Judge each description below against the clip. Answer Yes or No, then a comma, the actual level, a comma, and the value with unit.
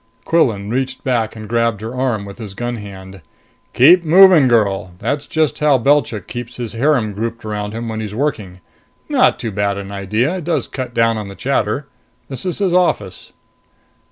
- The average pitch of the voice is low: Yes, low, 115 Hz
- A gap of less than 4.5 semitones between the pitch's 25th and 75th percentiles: No, average, 5.0 semitones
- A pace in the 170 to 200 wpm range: Yes, average, 180 wpm